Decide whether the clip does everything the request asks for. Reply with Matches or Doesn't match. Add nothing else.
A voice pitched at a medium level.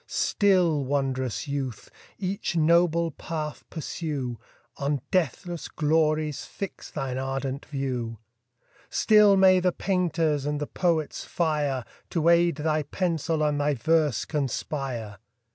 Matches